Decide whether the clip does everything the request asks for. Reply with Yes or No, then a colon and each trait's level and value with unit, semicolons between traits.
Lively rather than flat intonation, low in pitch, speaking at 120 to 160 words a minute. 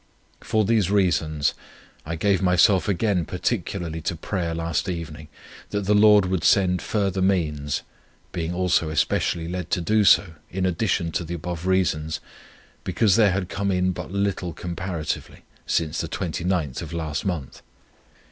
No: average, 2.9 semitones; very low, 90 Hz; average, 150 wpm